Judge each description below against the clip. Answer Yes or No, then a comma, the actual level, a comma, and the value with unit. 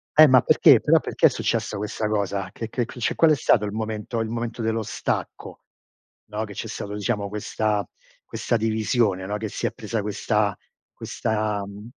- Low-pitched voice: Yes, low, 110 Hz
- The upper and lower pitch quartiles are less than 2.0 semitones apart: Yes, narrow, 1.6 semitones